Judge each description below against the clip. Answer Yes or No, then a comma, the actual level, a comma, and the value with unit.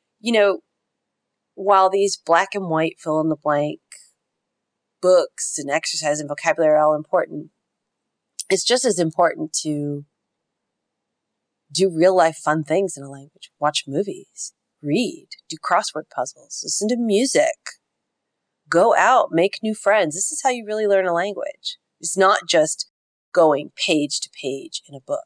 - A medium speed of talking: Yes, average, 150 wpm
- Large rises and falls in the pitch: Yes, wide, 6.2 semitones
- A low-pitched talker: No, medium, 180 Hz